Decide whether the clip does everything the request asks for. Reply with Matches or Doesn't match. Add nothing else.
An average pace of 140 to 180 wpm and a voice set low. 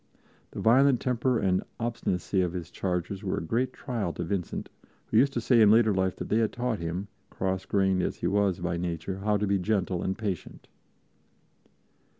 Doesn't match